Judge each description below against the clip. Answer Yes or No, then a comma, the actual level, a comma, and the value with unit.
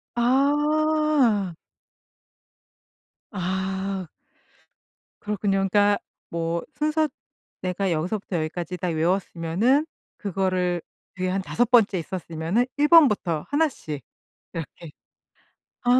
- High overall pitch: Yes, high, 195 Hz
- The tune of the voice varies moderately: No, wide, 6.0 semitones